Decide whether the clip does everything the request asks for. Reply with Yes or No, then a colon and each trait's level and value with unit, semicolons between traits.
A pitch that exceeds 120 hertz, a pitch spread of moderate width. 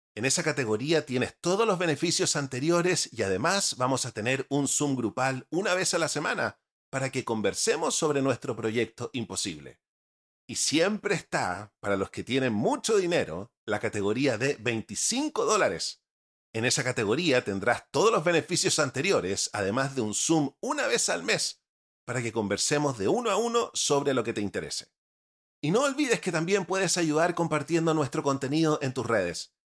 No: low, 135 Hz; wide, 6.3 semitones